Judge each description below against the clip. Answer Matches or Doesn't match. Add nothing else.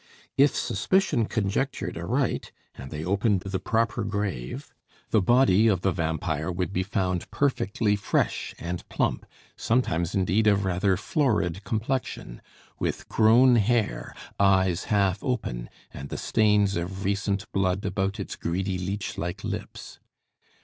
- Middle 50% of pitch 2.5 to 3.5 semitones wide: Matches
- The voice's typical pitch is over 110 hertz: Doesn't match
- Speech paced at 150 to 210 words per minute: Doesn't match